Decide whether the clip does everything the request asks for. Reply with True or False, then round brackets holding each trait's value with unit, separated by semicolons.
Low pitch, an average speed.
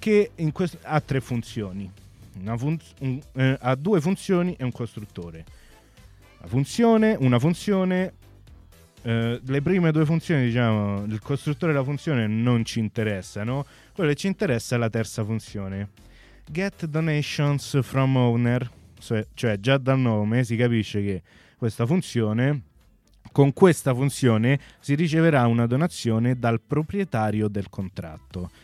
True (120 Hz; 140 wpm)